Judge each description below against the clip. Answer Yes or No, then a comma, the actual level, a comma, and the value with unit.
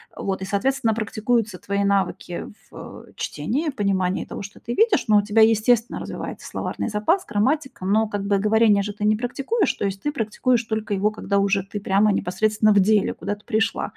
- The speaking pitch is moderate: No, high, 210 Hz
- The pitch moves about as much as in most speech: No, narrow, 2.3 semitones